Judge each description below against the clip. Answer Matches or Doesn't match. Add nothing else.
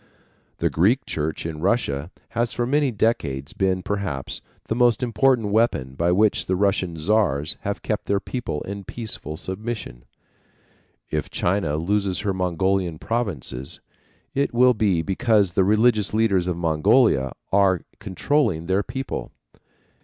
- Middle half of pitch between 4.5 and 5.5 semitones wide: Matches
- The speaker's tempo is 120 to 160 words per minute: Matches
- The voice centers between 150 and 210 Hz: Doesn't match